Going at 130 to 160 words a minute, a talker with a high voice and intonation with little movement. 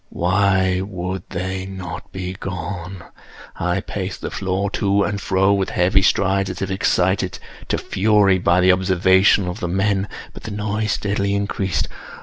No: average, 150 wpm; very low, 95 Hz; narrow, 1.4 semitones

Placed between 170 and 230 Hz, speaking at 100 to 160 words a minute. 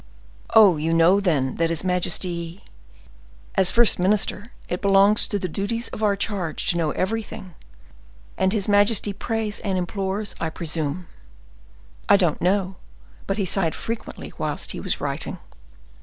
Yes: high, 190 Hz; average, 150 wpm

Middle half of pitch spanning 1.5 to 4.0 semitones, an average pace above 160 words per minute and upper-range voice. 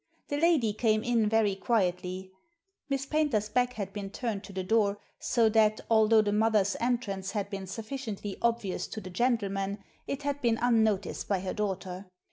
Yes: average, 3.2 semitones; average, 170 wpm; high, 215 Hz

